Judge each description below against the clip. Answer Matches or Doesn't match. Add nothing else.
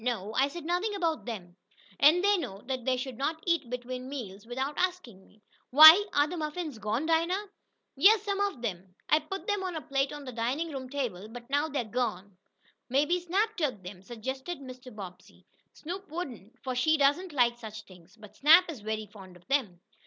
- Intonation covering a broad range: Matches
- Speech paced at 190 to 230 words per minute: Matches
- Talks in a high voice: Matches